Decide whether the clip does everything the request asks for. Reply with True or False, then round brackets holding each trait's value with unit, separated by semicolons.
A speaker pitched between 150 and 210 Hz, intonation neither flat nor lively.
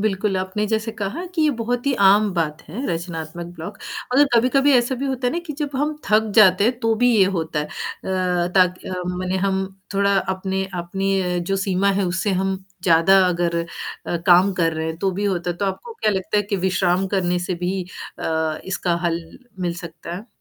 True (190 Hz; 3.6 semitones)